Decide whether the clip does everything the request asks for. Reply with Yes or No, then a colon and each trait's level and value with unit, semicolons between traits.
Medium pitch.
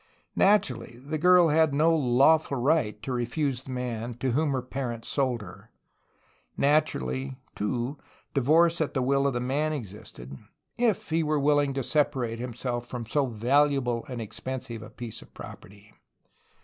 No: low, 130 Hz